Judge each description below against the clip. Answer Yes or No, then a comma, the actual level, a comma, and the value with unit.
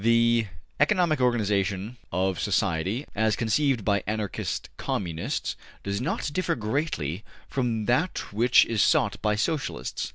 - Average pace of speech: No, slow, 125 wpm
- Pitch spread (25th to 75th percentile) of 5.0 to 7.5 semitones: No, average, 4.3 semitones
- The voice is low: Yes, low, 110 Hz